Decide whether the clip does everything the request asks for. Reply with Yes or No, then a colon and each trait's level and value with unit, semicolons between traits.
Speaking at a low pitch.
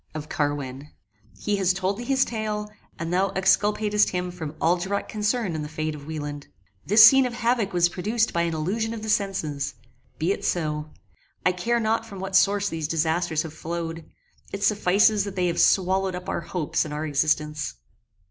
No: medium, 180 Hz